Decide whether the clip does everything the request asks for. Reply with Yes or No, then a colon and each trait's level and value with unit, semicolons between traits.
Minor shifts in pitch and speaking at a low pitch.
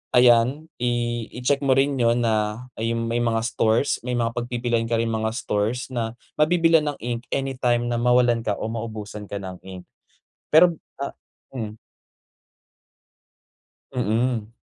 Yes: narrow, 1.9 semitones; low, 120 Hz